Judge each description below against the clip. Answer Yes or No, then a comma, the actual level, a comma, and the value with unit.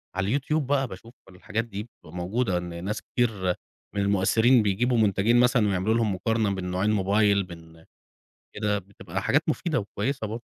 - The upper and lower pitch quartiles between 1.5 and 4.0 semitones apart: Yes, average, 3.6 semitones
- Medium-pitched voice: No, low, 105 Hz